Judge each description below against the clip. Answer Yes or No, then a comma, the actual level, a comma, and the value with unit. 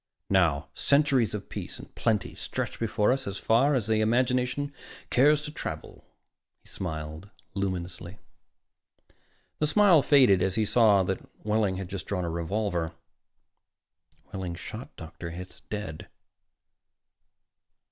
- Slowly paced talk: Yes, slow, 125 wpm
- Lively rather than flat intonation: Yes, wide, 5.8 semitones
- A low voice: Yes, low, 105 Hz